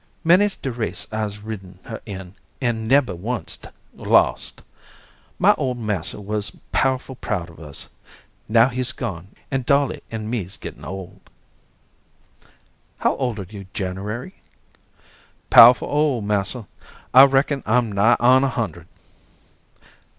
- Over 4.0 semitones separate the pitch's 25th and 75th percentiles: Yes, average, 4.5 semitones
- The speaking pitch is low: Yes, low, 110 Hz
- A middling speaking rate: No, slow, 130 wpm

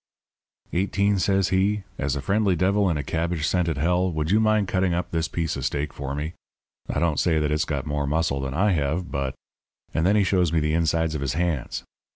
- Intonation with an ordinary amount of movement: Yes, average, 3.8 semitones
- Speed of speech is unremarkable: No, fast, 225 wpm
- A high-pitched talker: No, very low, 85 Hz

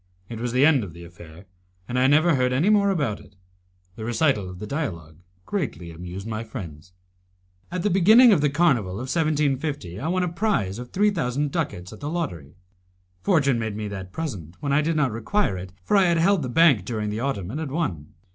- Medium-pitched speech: No, low, 130 Hz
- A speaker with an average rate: No, fast, 215 wpm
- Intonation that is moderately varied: No, wide, 8.6 semitones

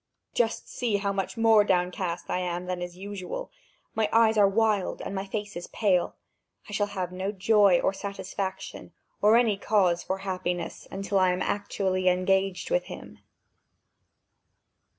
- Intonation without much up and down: Yes, narrow, 2.2 semitones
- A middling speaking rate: Yes, average, 155 wpm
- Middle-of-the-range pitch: No, high, 195 Hz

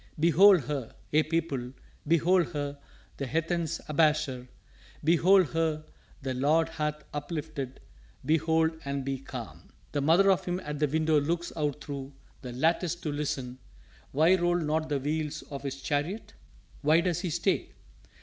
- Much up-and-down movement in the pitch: No, average, 2.7 semitones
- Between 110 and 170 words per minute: Yes, average, 150 wpm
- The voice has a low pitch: No, medium, 155 Hz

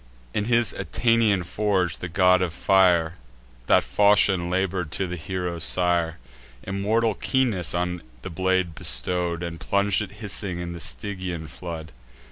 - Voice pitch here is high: No, very low, 90 Hz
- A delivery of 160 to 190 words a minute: No, average, 140 wpm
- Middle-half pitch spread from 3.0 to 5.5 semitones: No, narrow, 2.5 semitones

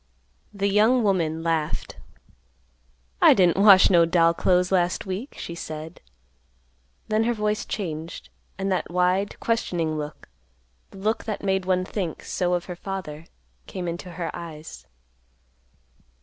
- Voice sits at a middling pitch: Yes, medium, 180 Hz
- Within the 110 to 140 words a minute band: Yes, slow, 135 wpm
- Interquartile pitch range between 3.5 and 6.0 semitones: No, average, 2.9 semitones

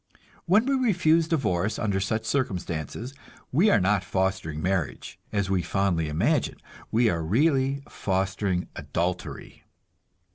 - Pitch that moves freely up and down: Yes, wide, 7.2 semitones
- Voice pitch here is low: Yes, low, 100 Hz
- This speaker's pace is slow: Yes, slow, 120 wpm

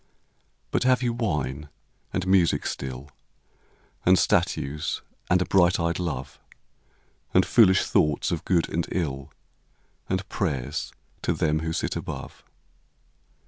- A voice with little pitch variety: No, average, 3.9 semitones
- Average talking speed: No, slow, 125 wpm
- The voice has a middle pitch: No, very low, 85 Hz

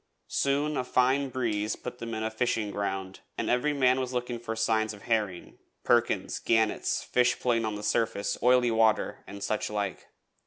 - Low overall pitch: Yes, low, 115 Hz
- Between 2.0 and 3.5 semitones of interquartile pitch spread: Yes, average, 2.8 semitones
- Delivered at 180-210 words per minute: Yes, average, 185 wpm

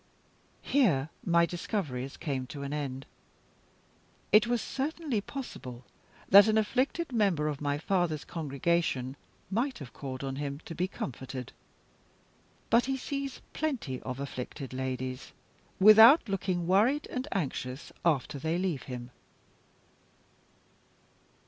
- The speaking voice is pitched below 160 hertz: No, medium, 165 Hz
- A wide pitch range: Yes, wide, 8.4 semitones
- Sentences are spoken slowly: Yes, slow, 120 wpm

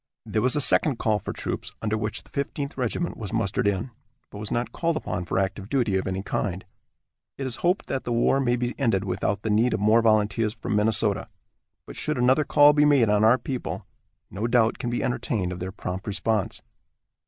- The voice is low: Yes, low, 110 Hz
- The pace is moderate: No, fast, 220 wpm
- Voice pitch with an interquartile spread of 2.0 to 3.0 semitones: No, average, 3.7 semitones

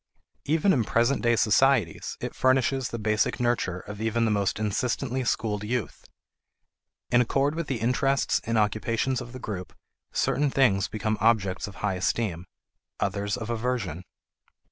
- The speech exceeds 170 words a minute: No, average, 150 wpm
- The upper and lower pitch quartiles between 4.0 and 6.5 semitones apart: No, average, 3.5 semitones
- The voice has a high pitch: No, low, 115 Hz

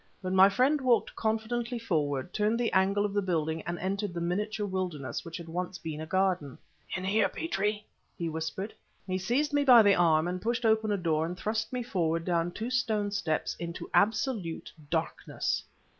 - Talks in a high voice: Yes, high, 195 Hz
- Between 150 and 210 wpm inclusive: Yes, average, 185 wpm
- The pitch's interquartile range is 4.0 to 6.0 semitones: Yes, average, 4.4 semitones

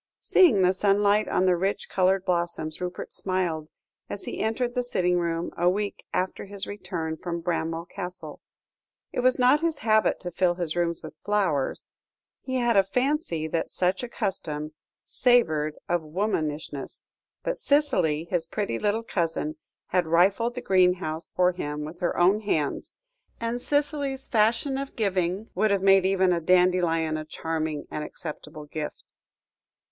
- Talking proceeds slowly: No, average, 155 wpm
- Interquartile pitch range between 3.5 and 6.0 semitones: Yes, average, 4.3 semitones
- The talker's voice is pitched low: No, medium, 185 Hz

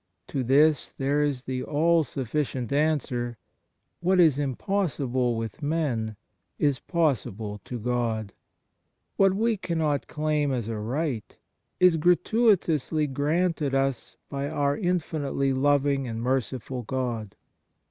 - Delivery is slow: Yes, slow, 115 wpm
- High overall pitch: No, medium, 140 Hz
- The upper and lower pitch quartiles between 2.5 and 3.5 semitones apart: No, average, 4.2 semitones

